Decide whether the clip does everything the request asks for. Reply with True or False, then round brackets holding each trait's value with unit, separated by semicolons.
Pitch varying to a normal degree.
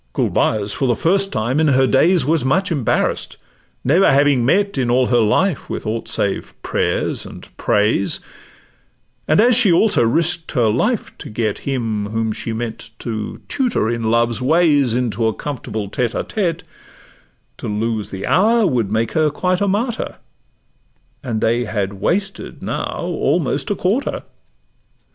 False (7.7 semitones)